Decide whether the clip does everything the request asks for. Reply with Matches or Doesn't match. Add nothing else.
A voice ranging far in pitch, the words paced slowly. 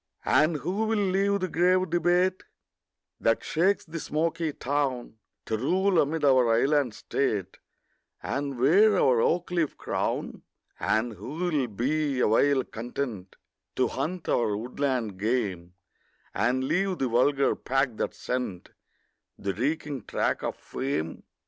Matches